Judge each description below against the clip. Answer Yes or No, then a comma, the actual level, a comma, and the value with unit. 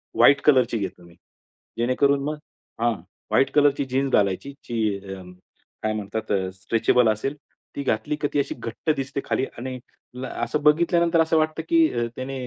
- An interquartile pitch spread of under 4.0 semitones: No, average, 4.8 semitones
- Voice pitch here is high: No, low, 130 Hz